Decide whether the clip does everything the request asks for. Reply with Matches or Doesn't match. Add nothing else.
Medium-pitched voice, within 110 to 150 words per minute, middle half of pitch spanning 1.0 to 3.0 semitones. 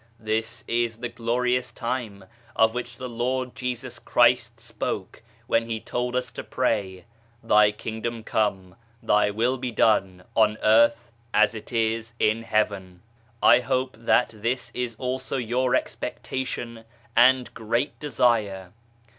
Doesn't match